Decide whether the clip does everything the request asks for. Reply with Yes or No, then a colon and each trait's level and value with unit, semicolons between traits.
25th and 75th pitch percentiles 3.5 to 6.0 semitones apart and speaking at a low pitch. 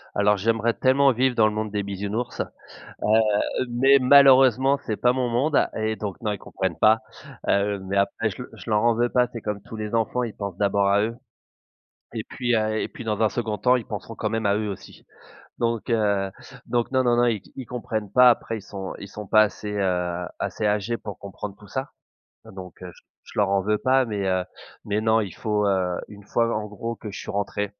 No: average, 2.8 semitones; low, 110 Hz